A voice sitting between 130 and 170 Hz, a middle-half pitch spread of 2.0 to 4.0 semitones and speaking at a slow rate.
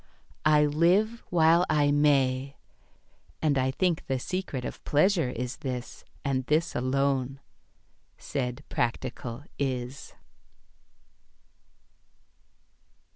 Yes: medium, 140 Hz; average, 3.2 semitones; slow, 90 wpm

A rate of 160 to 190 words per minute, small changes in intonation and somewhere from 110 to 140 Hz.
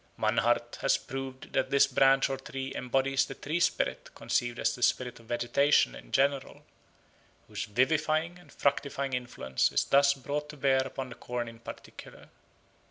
Yes: average, 165 wpm; narrow, 2.2 semitones; low, 135 Hz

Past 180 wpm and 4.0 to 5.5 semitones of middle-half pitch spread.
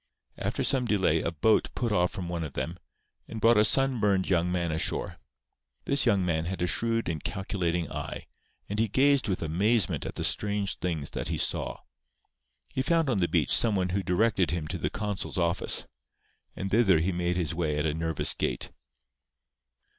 Yes: average, 190 wpm; average, 4.5 semitones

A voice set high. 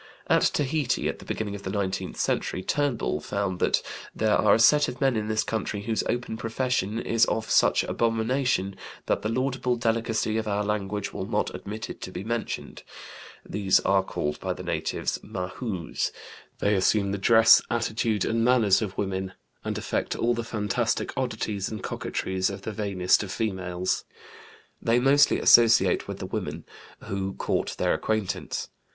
No: low, 110 Hz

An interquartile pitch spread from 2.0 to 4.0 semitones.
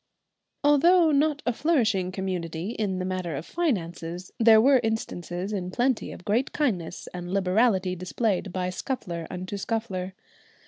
No: average, 5.1 semitones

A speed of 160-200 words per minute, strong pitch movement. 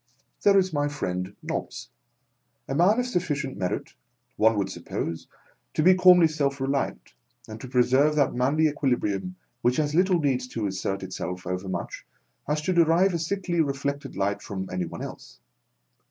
Yes: average, 170 wpm; wide, 8.1 semitones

